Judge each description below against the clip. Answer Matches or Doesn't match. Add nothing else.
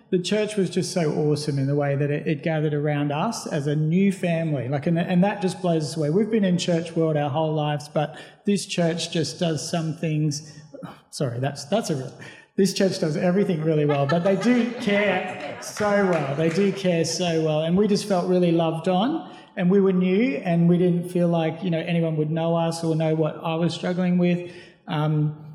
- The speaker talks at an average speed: Doesn't match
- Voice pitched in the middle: Matches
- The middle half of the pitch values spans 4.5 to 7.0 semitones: Doesn't match